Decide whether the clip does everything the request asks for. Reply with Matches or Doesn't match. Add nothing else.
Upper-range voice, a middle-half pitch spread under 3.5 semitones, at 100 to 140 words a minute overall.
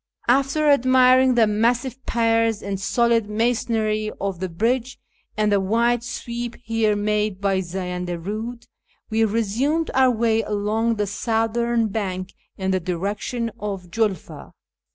Matches